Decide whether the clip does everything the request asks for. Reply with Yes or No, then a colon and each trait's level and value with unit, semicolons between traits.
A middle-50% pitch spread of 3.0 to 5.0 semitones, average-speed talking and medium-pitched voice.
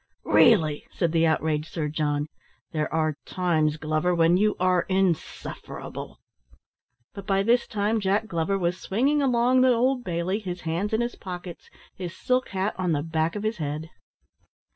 Yes: average, 4.7 semitones; average, 165 wpm; medium, 180 Hz